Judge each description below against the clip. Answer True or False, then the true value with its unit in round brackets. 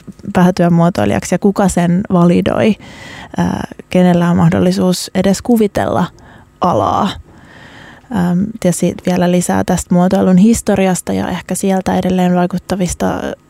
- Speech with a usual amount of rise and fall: False (1.4 semitones)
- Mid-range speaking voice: True (180 Hz)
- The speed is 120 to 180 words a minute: False (105 wpm)